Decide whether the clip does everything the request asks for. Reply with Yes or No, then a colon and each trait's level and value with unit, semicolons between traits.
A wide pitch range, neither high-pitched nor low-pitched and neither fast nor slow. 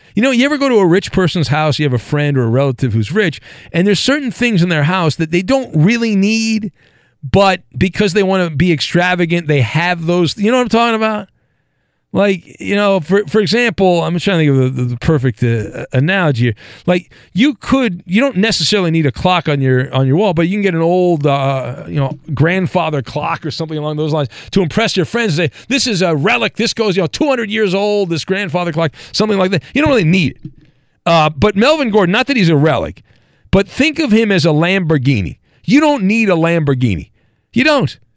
No: wide, 5.9 semitones; medium, 175 Hz; fast, 230 wpm